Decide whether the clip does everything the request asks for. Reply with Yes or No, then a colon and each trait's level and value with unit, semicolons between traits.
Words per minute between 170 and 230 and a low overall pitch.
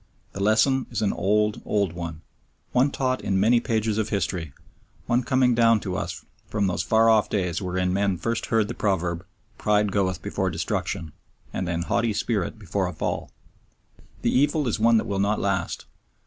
Yes: average, 180 wpm; low, 100 Hz